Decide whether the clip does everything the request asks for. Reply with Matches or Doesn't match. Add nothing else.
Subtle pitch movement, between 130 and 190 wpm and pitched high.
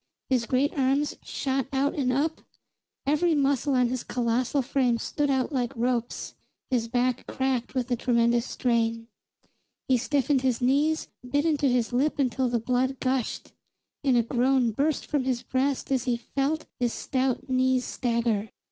Matches